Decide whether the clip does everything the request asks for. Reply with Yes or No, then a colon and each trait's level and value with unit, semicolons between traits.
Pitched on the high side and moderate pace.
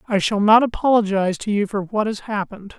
No: high, 205 Hz; fast, 215 wpm